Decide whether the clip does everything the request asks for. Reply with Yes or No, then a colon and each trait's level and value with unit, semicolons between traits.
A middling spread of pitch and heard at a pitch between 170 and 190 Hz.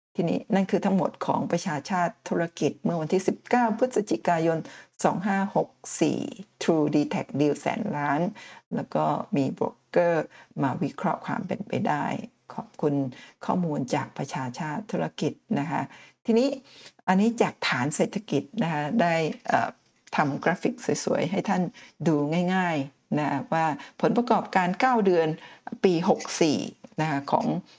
No: wide, 6.3 semitones; medium, 185 Hz